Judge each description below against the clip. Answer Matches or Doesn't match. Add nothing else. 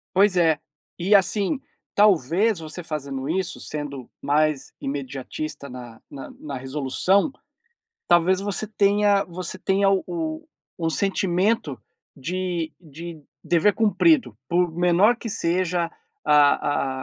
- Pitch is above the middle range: Doesn't match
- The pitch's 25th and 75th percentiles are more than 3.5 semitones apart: Matches